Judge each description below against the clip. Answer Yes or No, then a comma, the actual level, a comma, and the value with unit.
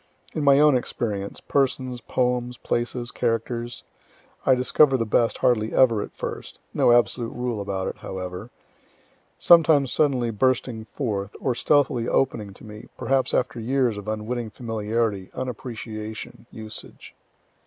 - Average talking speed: No, slow, 130 wpm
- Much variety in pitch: No, average, 2.9 semitones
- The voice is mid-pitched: No, low, 120 Hz